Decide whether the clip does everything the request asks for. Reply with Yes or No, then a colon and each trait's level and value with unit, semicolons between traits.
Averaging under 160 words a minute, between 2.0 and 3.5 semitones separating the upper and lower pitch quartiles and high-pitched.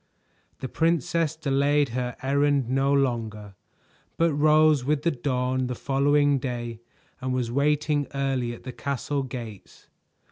No: slow, 135 wpm; average, 2.7 semitones; low, 135 Hz